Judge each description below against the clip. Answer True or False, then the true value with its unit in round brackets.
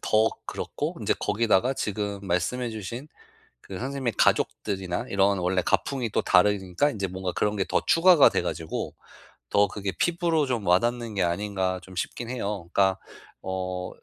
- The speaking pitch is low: True (100 Hz)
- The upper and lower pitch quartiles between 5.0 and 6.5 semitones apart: False (4.3 semitones)